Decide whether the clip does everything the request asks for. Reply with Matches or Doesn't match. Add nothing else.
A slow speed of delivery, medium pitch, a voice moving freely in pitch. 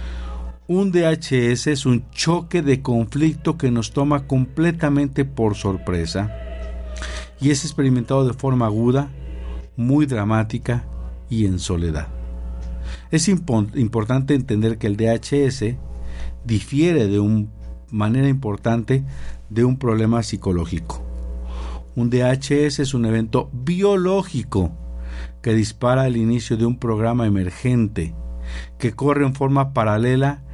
Doesn't match